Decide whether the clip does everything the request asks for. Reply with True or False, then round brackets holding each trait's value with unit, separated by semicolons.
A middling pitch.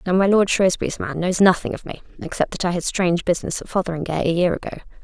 True (180 Hz)